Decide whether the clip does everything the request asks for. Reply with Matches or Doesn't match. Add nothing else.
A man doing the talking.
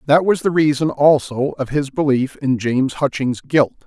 Matches